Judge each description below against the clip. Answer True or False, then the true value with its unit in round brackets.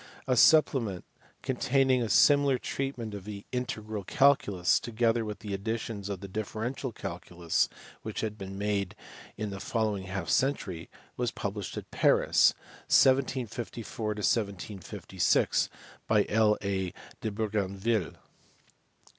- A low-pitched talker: True (110 Hz)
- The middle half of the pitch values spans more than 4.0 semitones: False (3.7 semitones)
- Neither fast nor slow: False (115 wpm)